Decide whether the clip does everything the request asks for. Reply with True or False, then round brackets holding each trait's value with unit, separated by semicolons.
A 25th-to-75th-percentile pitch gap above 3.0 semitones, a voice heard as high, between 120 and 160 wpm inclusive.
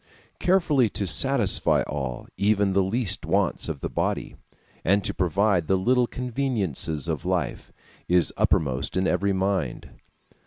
False (5.1 semitones; 100 Hz; 140 wpm)